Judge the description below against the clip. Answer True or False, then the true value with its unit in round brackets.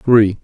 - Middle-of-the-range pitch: False (110 Hz)